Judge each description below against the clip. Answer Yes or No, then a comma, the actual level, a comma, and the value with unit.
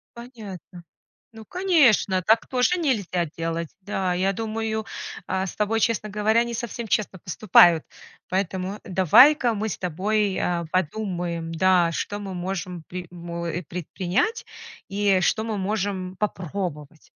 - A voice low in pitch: No, high, 190 Hz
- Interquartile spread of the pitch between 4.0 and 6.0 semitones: No, average, 3.6 semitones